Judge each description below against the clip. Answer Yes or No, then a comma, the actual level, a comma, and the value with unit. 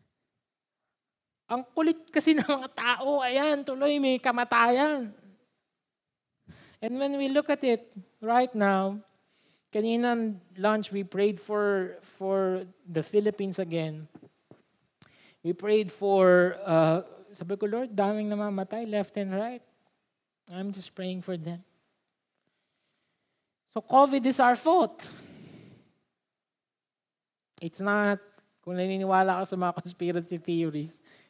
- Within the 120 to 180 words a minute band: No, slow, 110 wpm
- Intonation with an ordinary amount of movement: Yes, average, 4.5 semitones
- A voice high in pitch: Yes, high, 205 Hz